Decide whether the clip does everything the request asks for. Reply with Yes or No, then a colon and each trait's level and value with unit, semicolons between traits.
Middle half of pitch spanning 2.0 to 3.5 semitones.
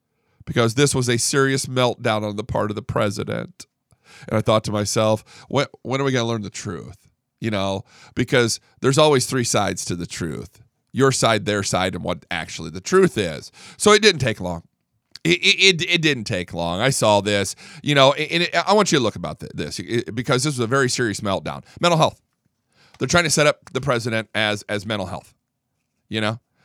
No: average, 4.6 semitones